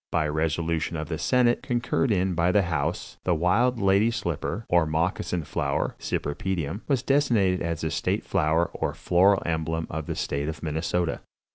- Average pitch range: Yes, average, 3.8 semitones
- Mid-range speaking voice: No, very low, 85 Hz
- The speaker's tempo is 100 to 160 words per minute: No, average, 170 wpm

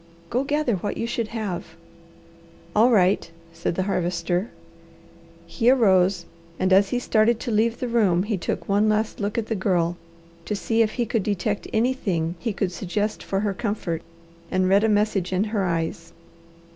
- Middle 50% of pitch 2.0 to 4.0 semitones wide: Yes, average, 3.4 semitones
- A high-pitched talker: Yes, high, 205 Hz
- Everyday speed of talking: Yes, average, 175 wpm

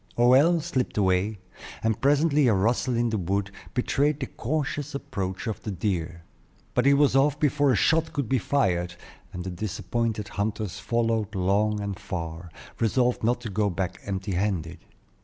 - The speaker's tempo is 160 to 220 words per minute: Yes, average, 165 wpm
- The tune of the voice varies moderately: No, wide, 5.8 semitones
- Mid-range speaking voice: No, low, 110 Hz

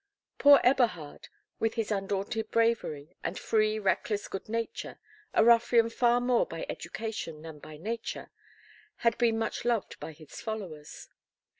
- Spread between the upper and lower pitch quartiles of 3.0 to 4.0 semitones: No, average, 4.8 semitones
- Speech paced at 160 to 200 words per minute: No, average, 140 wpm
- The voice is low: No, high, 220 Hz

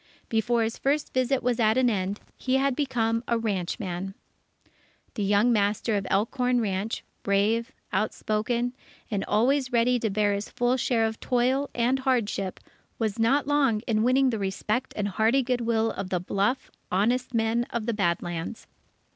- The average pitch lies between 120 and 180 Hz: No, high, 230 Hz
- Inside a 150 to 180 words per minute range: Yes, average, 165 wpm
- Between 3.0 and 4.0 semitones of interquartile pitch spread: Yes, average, 3.4 semitones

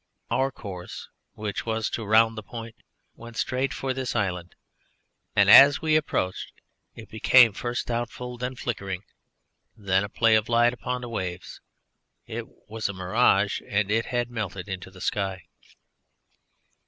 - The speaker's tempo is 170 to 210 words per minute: No, average, 150 wpm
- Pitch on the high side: No, low, 110 Hz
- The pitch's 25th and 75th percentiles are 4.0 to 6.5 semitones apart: No, average, 3.6 semitones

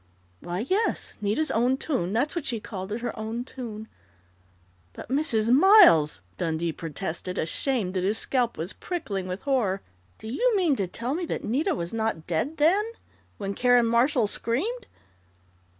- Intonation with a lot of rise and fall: Yes, wide, 7.0 semitones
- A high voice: Yes, high, 225 Hz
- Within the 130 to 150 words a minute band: No, average, 165 wpm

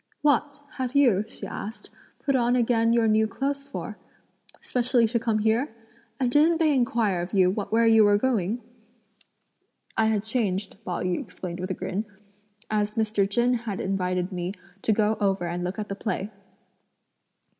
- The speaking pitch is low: No, high, 220 Hz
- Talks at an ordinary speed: Yes, average, 165 wpm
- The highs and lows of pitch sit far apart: No, average, 3.7 semitones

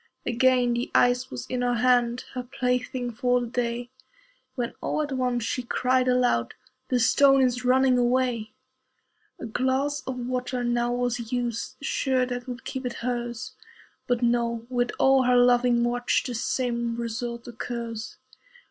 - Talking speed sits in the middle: Yes, average, 155 wpm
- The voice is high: Yes, high, 245 Hz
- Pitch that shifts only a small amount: Yes, narrow, 1.0 semitones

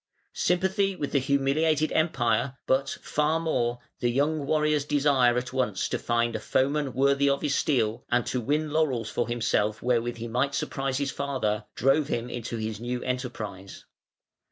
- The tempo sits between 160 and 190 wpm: Yes, average, 165 wpm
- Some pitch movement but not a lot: Yes, average, 3.5 semitones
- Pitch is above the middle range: No, low, 130 Hz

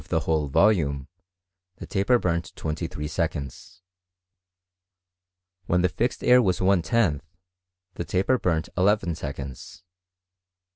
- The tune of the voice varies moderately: Yes, average, 4.6 semitones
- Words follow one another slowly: Yes, slow, 130 wpm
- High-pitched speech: No, very low, 85 Hz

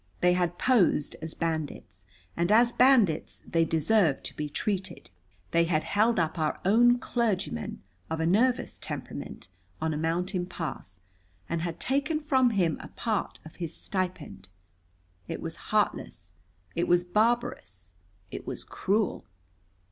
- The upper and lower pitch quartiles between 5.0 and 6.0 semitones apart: Yes, wide, 5.6 semitones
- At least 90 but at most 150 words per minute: Yes, average, 140 wpm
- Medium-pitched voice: Yes, medium, 180 Hz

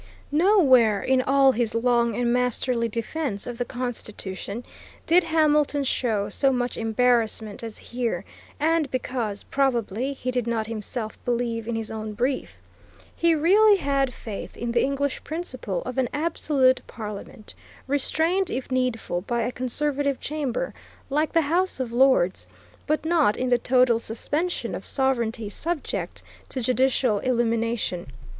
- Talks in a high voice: Yes, very high, 250 Hz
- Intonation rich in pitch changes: No, average, 3.7 semitones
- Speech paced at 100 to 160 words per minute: Yes, average, 140 wpm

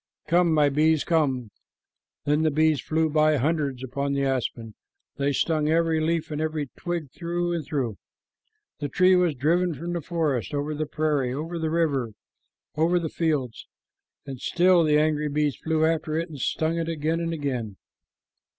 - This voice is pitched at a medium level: Yes, medium, 155 Hz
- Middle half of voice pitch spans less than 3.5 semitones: Yes, average, 2.7 semitones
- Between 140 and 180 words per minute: Yes, average, 170 wpm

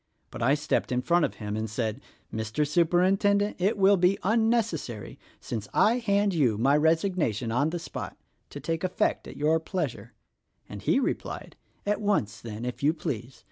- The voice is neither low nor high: Yes, medium, 155 Hz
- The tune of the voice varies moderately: No, wide, 8.4 semitones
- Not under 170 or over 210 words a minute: Yes, average, 180 wpm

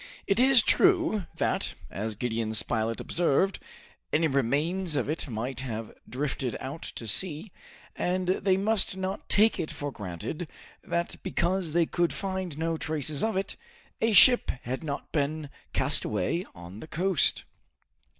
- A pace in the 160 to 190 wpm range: No, average, 145 wpm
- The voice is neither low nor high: Yes, medium, 160 Hz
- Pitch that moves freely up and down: Yes, wide, 6.4 semitones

